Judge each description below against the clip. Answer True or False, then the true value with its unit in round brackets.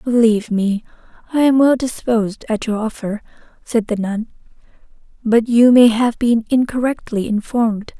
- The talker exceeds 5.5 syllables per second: False (4.9 syllables/s)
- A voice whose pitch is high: True (230 Hz)